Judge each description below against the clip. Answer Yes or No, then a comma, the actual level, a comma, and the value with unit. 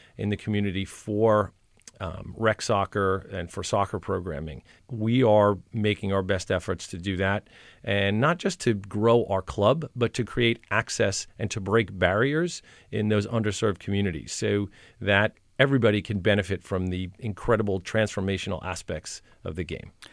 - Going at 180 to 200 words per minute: No, average, 155 wpm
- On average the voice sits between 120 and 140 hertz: No, low, 105 Hz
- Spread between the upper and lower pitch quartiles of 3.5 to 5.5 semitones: No, narrow, 2.6 semitones